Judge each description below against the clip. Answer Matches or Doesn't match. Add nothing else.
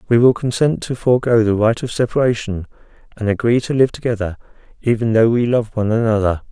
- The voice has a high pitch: Doesn't match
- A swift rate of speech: Doesn't match